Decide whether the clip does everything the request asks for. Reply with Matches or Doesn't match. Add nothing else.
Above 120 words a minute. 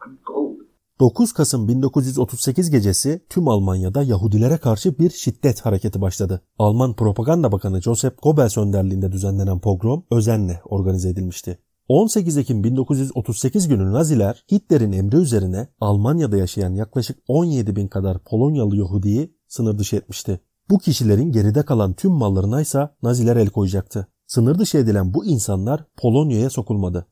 Matches